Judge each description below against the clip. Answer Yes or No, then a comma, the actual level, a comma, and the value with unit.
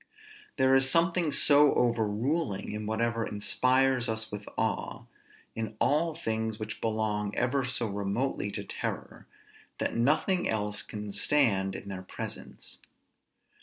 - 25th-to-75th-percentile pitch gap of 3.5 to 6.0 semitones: Yes, average, 4.3 semitones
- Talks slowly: Yes, slow, 130 wpm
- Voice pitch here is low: Yes, low, 115 Hz